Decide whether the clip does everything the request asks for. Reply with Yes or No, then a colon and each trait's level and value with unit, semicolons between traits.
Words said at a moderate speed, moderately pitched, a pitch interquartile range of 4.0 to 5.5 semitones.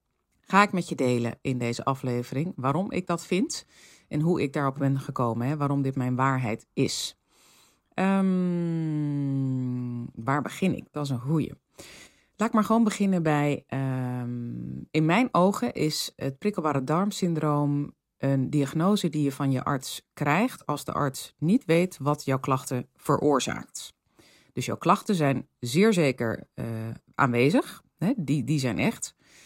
Yes: average, 155 wpm; medium, 145 Hz; average, 4.8 semitones